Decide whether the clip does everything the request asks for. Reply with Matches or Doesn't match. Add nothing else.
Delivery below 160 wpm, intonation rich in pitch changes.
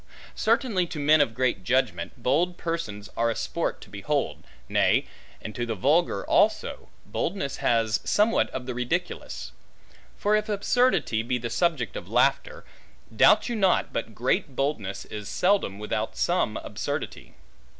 Matches